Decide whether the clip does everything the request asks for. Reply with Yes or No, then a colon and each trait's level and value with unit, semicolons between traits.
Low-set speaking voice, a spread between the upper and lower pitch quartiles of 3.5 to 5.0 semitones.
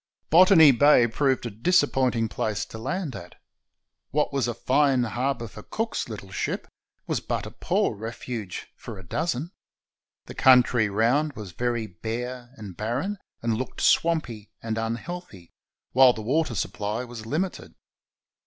Yes: low, 120 Hz; average, 4.6 semitones